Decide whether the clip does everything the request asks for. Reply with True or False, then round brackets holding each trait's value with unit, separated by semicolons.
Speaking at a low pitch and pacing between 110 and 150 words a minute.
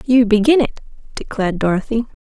False (225 Hz; 135 wpm)